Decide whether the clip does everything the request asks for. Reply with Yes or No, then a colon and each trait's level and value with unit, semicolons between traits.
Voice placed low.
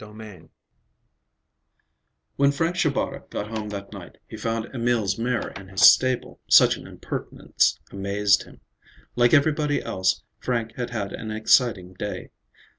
Yes: low, 110 Hz